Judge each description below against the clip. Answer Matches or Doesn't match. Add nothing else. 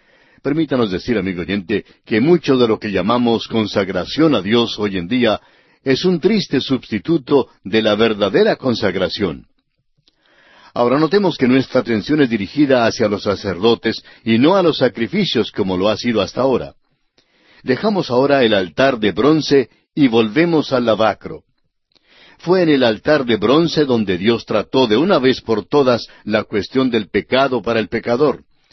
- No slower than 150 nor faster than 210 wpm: Matches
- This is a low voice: Matches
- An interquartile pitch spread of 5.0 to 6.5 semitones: Doesn't match